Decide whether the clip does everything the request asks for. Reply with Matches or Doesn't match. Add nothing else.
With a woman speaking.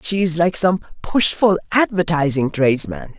Doesn't match